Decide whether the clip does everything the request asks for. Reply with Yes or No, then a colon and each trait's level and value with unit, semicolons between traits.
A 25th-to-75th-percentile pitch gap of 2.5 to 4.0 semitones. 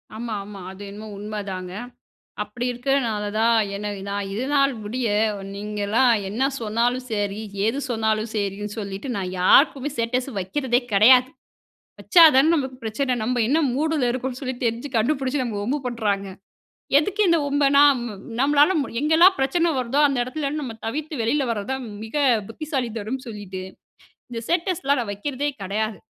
No: average, 4.7 semitones